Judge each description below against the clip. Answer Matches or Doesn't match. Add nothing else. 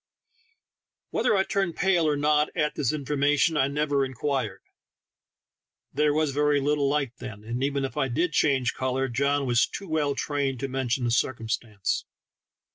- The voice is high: Doesn't match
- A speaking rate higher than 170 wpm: Doesn't match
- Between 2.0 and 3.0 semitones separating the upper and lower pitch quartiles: Matches